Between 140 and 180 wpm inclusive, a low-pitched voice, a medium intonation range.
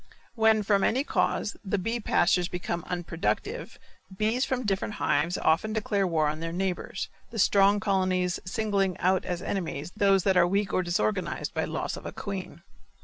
No: average, 175 wpm; high, 190 Hz; average, 3.0 semitones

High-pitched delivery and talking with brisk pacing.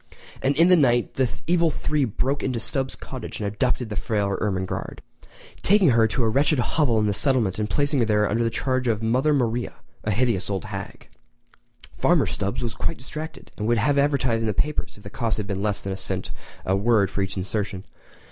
No: low, 115 Hz; fast, 215 wpm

